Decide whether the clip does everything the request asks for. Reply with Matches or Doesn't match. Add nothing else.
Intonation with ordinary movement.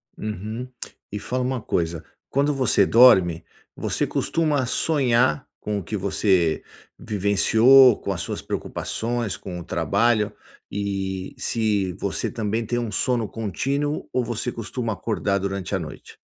Matches